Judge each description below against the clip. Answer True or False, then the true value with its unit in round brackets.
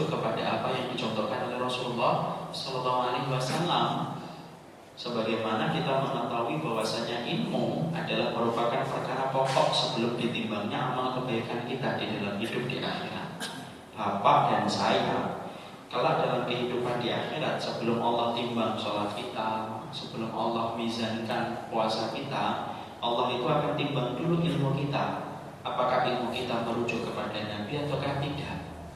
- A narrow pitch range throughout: True (2.3 semitones)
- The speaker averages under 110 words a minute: False (125 wpm)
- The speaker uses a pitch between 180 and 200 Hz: False (120 Hz)